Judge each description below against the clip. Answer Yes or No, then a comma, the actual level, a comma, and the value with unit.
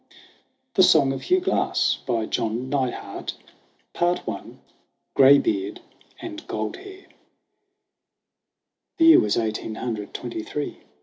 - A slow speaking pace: Yes, slow, 105 wpm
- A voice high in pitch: No, low, 135 Hz